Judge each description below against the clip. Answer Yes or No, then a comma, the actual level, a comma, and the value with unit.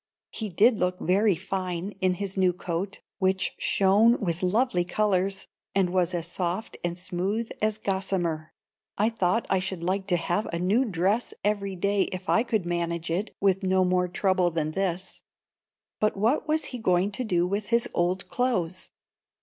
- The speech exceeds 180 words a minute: No, average, 175 wpm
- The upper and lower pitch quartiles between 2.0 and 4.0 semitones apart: Yes, narrow, 2.6 semitones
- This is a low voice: No, high, 190 Hz